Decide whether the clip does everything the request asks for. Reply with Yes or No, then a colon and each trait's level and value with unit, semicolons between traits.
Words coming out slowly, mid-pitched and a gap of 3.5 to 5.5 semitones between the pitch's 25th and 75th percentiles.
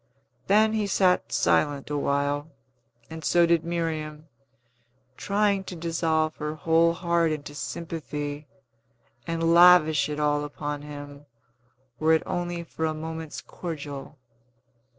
No: slow, 120 wpm; medium, 160 Hz; narrow, 2.4 semitones